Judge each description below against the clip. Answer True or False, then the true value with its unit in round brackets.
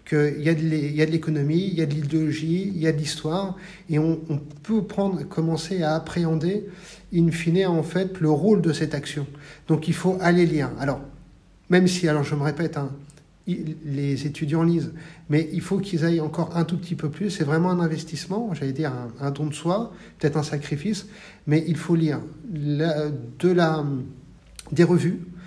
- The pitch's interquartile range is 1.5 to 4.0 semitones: True (2.7 semitones)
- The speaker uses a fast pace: False (195 wpm)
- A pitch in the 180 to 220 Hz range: False (160 Hz)